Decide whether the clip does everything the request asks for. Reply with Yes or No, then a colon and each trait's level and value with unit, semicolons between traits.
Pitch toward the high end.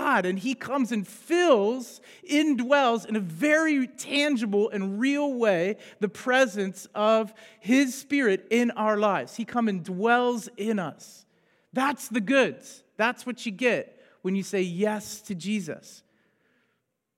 Yes: high, 225 Hz